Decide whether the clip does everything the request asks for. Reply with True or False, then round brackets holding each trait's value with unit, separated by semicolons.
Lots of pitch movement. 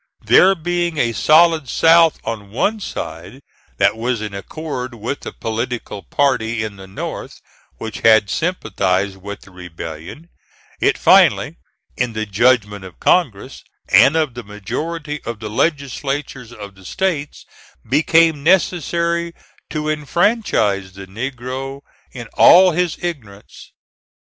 True (7.6 semitones)